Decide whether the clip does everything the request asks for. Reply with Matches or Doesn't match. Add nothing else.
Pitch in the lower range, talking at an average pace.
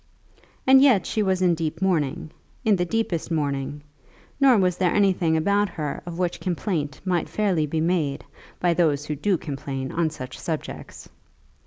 Doesn't match